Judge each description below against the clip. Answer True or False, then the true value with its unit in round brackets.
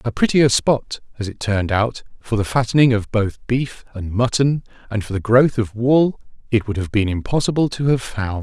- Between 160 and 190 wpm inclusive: False (205 wpm)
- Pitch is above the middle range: False (115 Hz)